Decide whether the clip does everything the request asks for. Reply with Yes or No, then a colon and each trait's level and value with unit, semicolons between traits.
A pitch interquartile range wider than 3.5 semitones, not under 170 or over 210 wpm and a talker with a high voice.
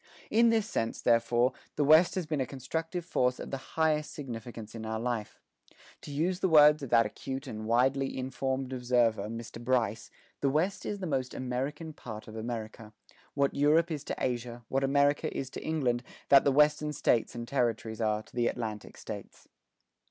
No: average, 4.3 semitones; average, 180 wpm; low, 130 Hz